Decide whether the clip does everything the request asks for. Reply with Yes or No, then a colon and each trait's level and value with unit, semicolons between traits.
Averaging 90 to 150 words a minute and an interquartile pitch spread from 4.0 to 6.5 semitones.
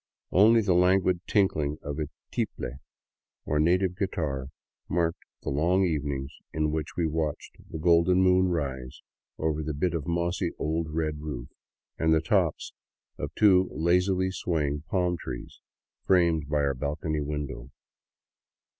No: average, 140 wpm; average, 3.5 semitones